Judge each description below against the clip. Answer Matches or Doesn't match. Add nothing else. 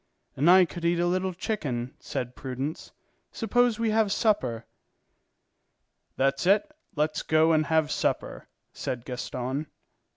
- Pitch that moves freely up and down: Matches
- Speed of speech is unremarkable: Doesn't match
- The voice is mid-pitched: Matches